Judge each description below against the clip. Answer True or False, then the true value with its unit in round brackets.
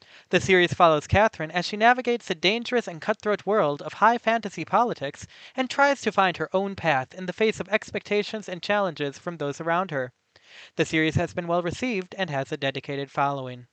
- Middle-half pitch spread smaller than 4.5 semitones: False (5.5 semitones)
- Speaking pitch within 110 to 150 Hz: False (180 Hz)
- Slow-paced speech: False (195 wpm)